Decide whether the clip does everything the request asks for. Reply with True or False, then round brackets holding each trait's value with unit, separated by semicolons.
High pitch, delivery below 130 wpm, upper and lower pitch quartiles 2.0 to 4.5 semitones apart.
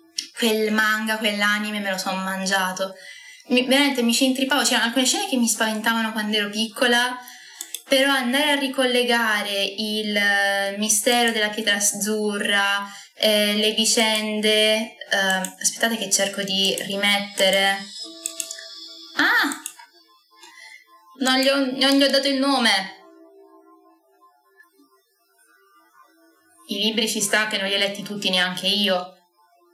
False (215 Hz; 120 wpm; 5.1 semitones)